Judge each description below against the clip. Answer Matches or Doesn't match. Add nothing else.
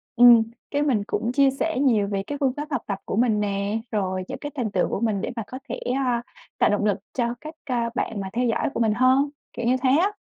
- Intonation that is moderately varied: Matches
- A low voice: Doesn't match